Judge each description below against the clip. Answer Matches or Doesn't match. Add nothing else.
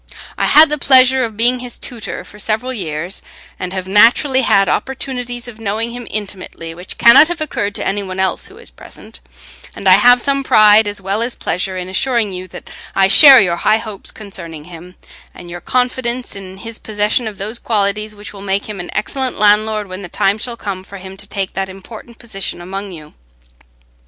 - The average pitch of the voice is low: Doesn't match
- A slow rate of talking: Doesn't match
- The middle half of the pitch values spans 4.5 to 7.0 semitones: Doesn't match